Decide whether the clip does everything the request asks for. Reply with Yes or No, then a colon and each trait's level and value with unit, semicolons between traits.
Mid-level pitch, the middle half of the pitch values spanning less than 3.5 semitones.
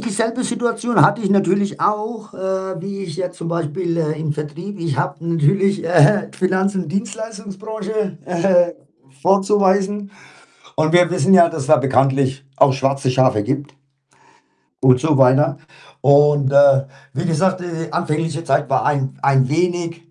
No: medium, 170 Hz; average, 5.0 semitones